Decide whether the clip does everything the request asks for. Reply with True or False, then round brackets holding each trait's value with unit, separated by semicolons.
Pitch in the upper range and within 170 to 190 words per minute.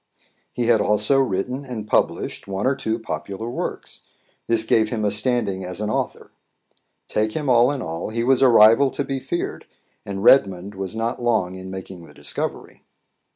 False (110 Hz; 180 wpm)